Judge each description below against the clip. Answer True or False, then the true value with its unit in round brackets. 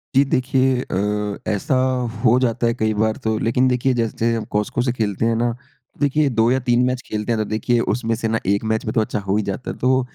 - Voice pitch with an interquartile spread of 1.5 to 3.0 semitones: True (2.7 semitones)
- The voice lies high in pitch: False (115 Hz)